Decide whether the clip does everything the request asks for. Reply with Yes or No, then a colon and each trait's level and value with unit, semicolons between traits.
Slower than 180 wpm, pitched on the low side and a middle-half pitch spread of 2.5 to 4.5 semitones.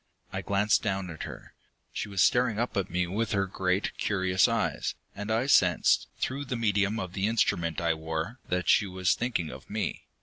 No: average, 195 wpm; low, 100 Hz; average, 3.5 semitones